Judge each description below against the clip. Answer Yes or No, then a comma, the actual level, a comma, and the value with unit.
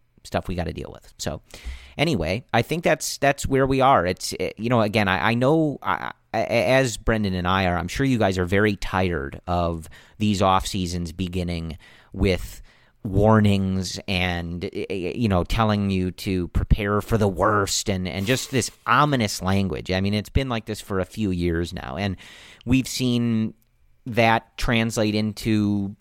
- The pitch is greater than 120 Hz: No, low, 100 Hz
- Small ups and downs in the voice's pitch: No, average, 3.8 semitones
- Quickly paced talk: No, average, 175 wpm